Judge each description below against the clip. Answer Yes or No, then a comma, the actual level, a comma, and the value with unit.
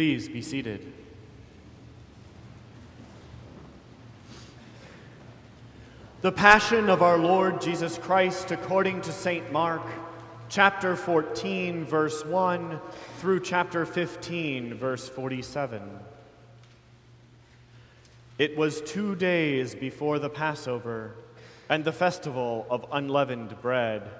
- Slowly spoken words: Yes, slow, 90 wpm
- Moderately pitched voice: Yes, medium, 145 Hz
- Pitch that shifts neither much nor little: No, wide, 6.5 semitones